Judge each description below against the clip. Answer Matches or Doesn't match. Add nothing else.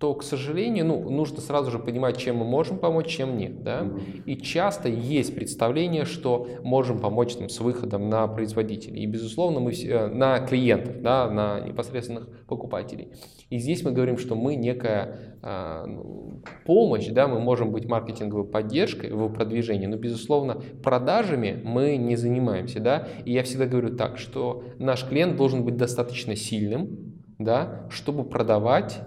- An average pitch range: Matches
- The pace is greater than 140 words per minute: Matches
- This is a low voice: Matches